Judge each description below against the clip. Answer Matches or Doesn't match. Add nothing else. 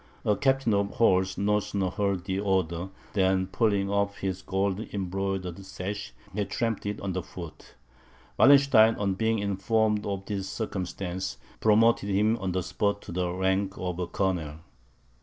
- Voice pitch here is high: Doesn't match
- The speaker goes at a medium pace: Matches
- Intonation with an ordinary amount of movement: Doesn't match